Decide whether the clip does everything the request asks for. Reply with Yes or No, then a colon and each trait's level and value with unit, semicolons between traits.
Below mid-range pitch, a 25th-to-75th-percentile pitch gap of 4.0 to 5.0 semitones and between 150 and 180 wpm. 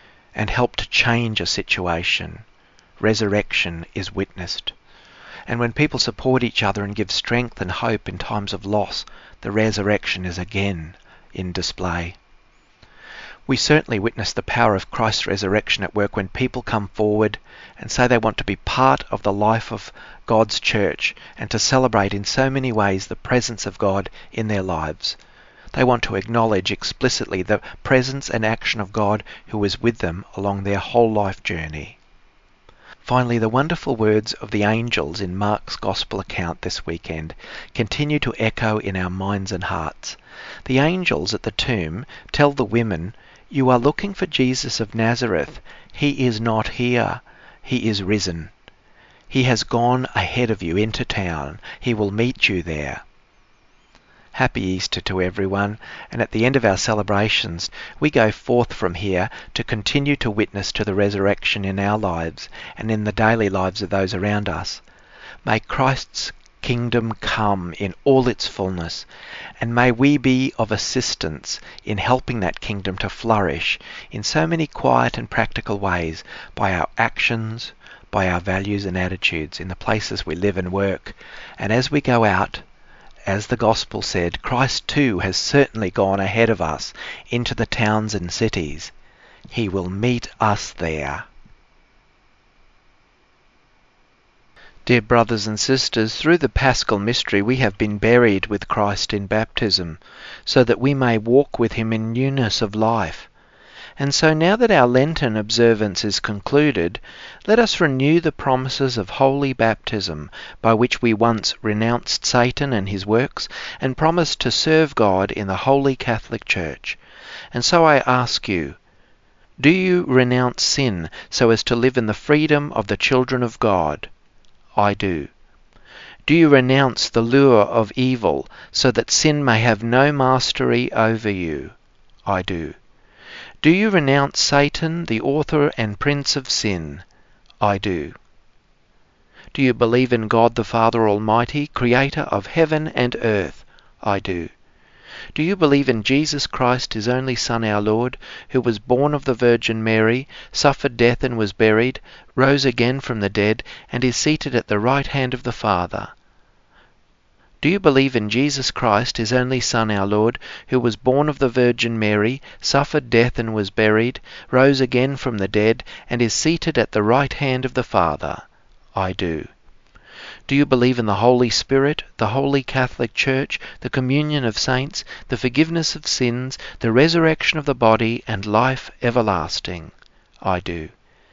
Yes: low, 115 Hz; average, 4.3 semitones; average, 160 wpm